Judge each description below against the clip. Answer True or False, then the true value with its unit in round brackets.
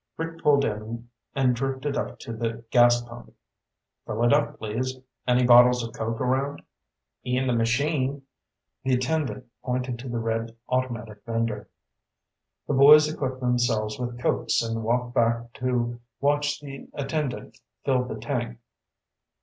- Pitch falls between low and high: False (125 Hz)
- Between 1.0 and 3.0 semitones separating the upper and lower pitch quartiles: True (2.6 semitones)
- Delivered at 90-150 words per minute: True (140 wpm)